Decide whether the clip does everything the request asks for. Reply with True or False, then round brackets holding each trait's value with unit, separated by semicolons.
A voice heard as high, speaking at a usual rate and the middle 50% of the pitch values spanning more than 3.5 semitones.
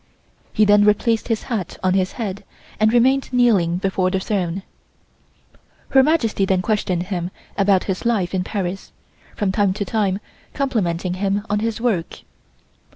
False (200 Hz; 155 wpm; 3.2 semitones)